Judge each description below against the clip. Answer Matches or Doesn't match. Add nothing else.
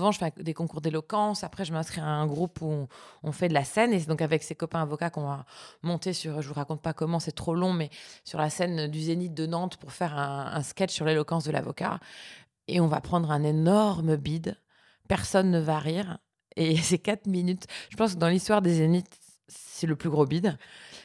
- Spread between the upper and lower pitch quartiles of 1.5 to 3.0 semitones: Matches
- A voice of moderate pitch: Matches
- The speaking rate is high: Matches